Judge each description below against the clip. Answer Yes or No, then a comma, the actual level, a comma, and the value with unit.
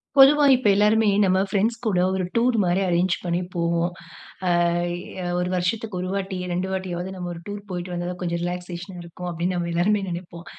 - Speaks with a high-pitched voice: No, medium, 180 Hz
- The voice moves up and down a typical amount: No, narrow, 2.2 semitones